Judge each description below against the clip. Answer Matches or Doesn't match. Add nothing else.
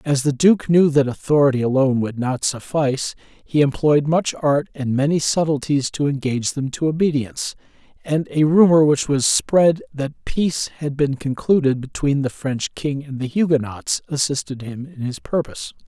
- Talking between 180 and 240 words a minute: Doesn't match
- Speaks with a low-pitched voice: Doesn't match